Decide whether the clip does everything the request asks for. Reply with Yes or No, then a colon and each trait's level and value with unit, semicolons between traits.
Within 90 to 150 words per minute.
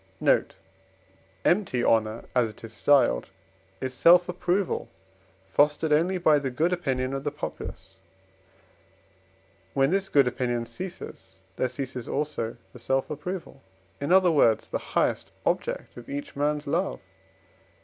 Yes: average, 140 wpm